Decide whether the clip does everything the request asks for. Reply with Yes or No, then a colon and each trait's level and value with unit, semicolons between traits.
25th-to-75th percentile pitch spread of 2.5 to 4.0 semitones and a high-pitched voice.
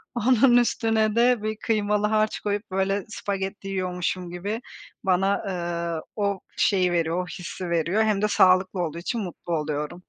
Yes: average, 3.2 semitones; high, 195 Hz